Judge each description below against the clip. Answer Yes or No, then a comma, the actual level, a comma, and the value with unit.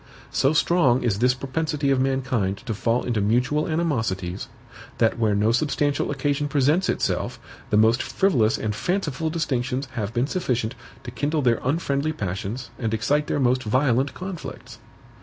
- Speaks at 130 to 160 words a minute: Yes, average, 155 wpm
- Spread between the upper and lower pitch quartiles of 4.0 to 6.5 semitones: Yes, average, 4.6 semitones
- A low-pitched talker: Yes, low, 130 Hz